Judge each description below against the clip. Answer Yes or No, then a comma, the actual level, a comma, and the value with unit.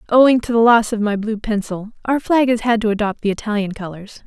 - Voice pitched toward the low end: No, high, 220 Hz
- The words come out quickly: Yes, fast, 240 wpm